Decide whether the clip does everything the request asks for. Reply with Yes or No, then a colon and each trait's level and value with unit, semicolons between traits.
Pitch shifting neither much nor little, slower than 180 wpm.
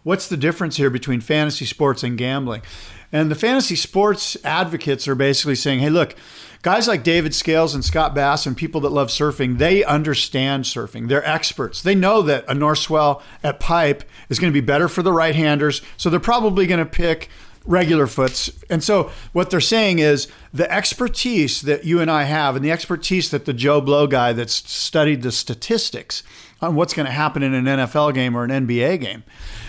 No: average, 4.0 semitones; average, 200 wpm